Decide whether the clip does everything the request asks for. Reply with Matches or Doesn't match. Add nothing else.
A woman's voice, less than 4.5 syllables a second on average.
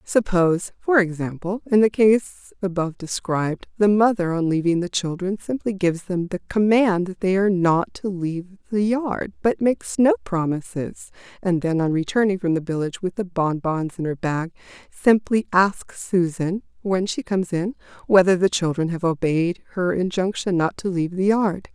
Doesn't match